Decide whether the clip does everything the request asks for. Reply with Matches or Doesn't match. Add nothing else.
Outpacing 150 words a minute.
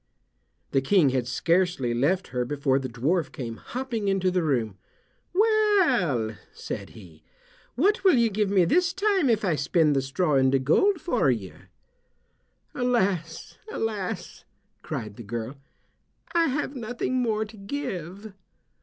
Doesn't match